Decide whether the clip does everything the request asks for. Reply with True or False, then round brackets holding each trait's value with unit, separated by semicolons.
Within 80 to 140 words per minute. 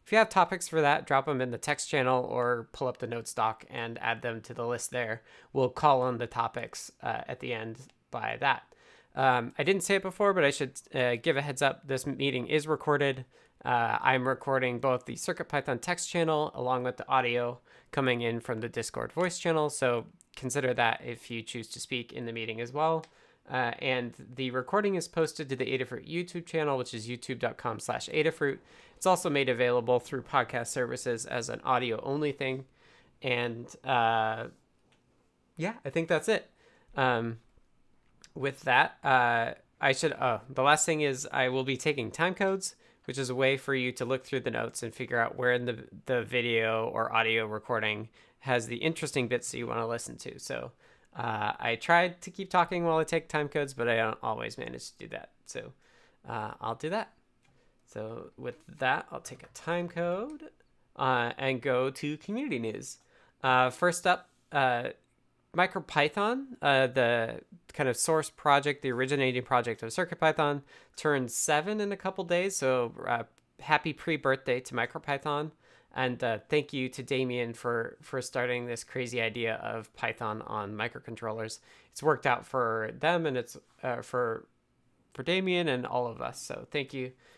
False (185 wpm)